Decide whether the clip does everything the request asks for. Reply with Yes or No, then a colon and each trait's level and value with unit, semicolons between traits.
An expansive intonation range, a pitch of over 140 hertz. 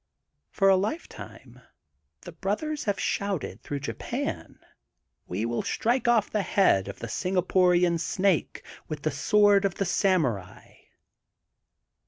Yes: wide, 5.7 semitones; high, 190 Hz